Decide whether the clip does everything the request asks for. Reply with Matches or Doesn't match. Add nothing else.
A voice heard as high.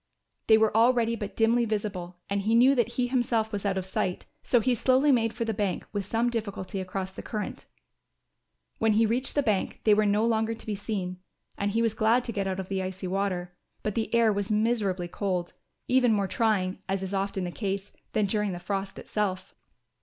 Matches